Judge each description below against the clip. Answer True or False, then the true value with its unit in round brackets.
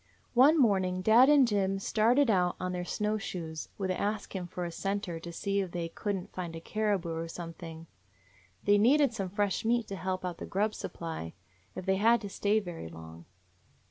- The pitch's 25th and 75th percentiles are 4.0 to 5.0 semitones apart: False (3.6 semitones)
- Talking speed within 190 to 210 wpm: True (205 wpm)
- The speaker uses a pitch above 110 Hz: True (190 Hz)